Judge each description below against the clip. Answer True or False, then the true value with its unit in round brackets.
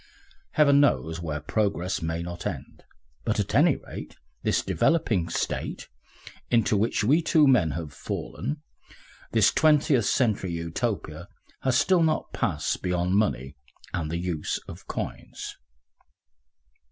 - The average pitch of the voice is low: True (100 Hz)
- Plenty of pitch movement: True (8.1 semitones)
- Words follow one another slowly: True (130 wpm)